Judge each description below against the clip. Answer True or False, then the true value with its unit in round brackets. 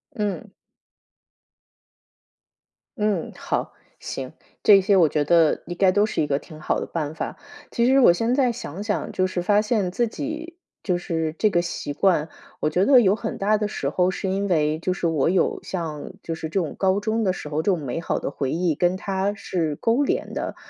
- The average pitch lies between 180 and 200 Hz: True (185 Hz)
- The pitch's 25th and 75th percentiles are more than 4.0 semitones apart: True (4.5 semitones)